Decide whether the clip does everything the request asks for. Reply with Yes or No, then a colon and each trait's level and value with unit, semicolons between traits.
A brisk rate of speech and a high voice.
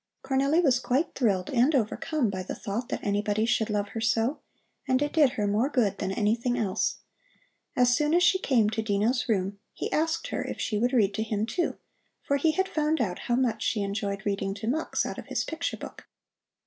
Yes: fast, 210 wpm; high, 235 Hz